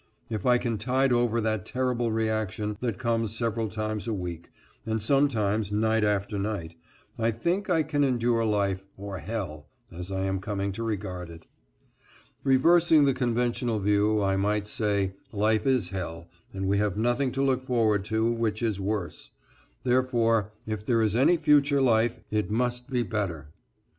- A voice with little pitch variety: No, average, 3.3 semitones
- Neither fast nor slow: Yes, average, 165 wpm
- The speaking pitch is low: Yes, low, 110 Hz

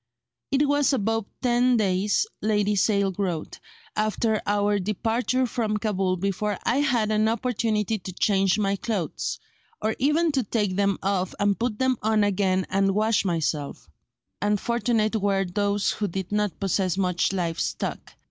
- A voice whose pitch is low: No, high, 205 Hz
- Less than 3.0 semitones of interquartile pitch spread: Yes, narrow, 2.5 semitones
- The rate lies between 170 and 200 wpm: No, average, 155 wpm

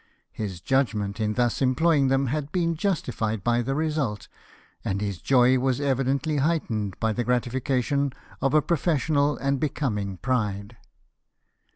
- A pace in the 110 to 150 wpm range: Yes, average, 140 wpm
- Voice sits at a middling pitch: No, low, 130 Hz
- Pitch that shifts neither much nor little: Yes, average, 4.5 semitones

